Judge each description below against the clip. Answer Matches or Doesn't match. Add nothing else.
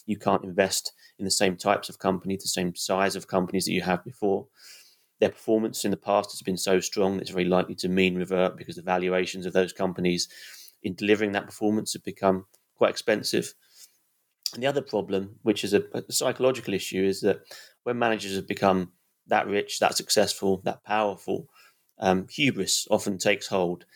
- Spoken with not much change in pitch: Matches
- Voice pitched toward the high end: Doesn't match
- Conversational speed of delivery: Matches